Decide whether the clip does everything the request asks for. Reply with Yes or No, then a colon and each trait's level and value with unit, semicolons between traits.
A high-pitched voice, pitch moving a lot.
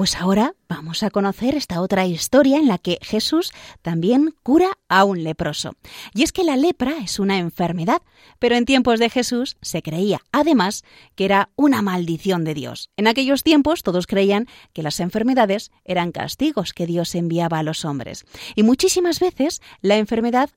Yes: high, 210 Hz; wide, 7.4 semitones